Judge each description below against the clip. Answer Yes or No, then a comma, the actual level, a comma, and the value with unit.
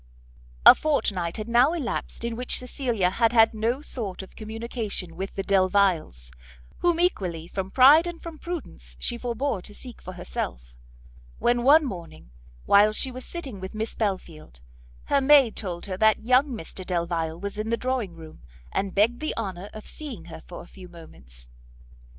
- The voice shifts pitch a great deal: Yes, wide, 5.8 semitones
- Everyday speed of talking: Yes, average, 175 wpm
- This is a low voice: No, high, 215 Hz